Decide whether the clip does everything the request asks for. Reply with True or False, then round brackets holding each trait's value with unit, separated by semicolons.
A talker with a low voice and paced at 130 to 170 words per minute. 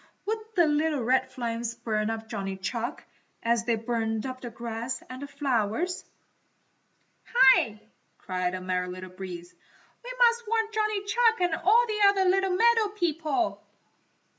False (255 Hz; 150 wpm)